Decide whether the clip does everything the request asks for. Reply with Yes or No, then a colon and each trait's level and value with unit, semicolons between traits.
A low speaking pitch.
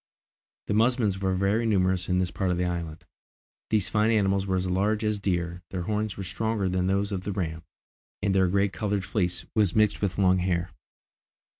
Yes: very low, 95 Hz